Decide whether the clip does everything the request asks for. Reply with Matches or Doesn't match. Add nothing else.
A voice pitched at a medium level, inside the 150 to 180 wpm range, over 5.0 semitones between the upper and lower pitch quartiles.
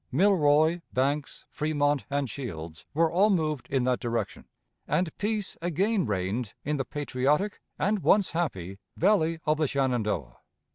Doesn't match